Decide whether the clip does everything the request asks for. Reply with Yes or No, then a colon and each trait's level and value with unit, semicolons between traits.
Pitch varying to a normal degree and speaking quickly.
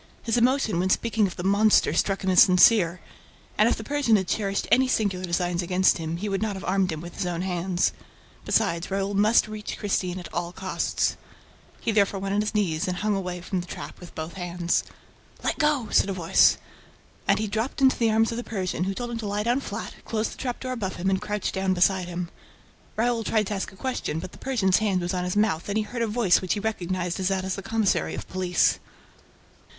Yes: average, 3.2 semitones; fast, 235 wpm